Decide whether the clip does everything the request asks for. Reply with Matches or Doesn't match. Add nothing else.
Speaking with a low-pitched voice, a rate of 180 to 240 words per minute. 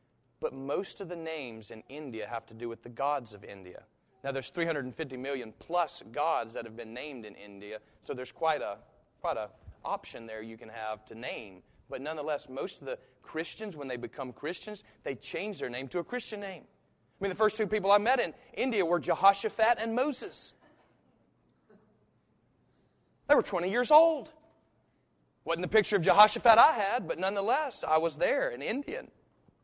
Doesn't match